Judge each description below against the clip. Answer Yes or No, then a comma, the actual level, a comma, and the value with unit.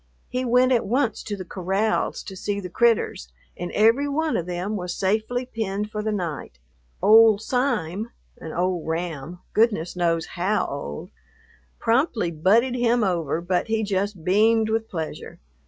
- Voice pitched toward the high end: Yes, high, 205 Hz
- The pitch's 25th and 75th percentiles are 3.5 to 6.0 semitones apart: Yes, average, 4.4 semitones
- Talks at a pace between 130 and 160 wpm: Yes, average, 155 wpm